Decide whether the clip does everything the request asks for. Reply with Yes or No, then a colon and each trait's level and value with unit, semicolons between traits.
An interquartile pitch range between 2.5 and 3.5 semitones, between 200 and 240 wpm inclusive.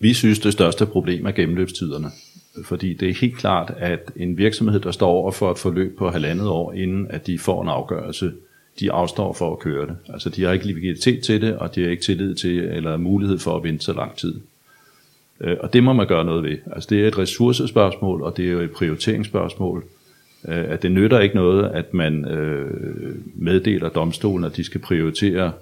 Yes: average, 2.9 semitones; average, 205 wpm